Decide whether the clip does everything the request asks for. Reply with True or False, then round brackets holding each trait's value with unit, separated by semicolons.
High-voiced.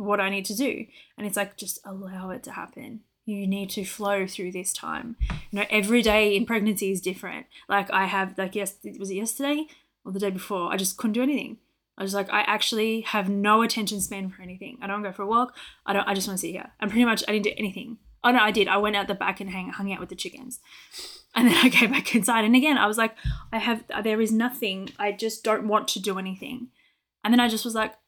True (210 Hz)